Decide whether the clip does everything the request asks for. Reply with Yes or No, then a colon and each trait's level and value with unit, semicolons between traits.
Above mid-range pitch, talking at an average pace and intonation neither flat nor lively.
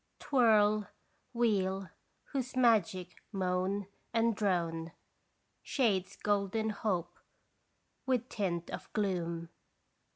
No: high, 200 Hz; slow, 85 wpm; average, 3.7 semitones